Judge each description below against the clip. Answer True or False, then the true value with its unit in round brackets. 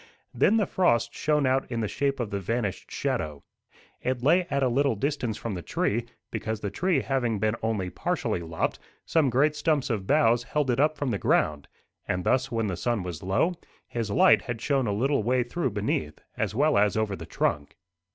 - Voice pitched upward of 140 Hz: False (120 Hz)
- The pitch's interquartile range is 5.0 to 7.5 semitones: True (5.3 semitones)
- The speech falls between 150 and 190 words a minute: False (205 wpm)